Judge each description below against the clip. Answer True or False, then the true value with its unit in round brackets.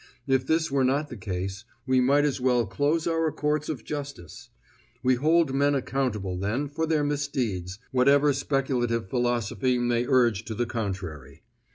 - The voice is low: True (130 Hz)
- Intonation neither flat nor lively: True (4.0 semitones)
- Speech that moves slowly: False (160 wpm)